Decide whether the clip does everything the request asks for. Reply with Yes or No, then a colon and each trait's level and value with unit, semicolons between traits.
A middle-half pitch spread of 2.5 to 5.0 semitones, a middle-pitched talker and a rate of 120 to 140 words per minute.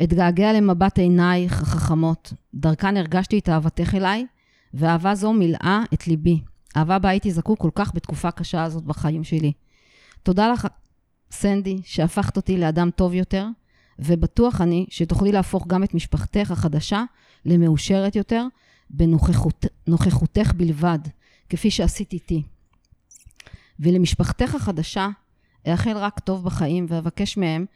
Yes: average, 3.4 semitones; medium, 175 Hz; average, 125 wpm